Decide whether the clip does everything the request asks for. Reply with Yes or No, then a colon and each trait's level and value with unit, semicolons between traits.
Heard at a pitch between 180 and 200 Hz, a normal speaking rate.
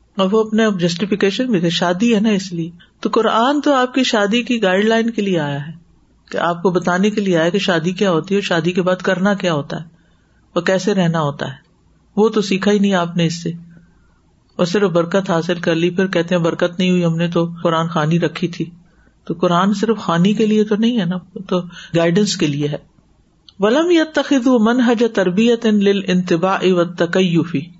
No: medium, 185 Hz; fast, 205 wpm